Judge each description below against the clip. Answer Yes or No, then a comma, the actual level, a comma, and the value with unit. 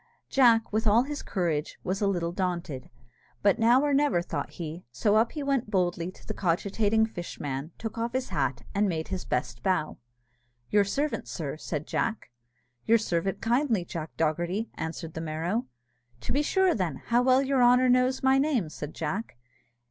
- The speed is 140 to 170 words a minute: No, average, 180 wpm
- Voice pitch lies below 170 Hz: No, high, 200 Hz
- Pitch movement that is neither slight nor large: No, wide, 6.6 semitones